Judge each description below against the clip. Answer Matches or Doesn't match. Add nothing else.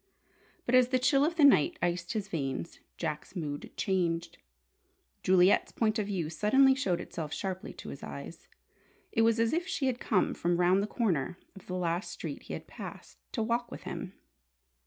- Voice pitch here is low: Doesn't match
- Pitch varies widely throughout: Matches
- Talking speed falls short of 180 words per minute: Doesn't match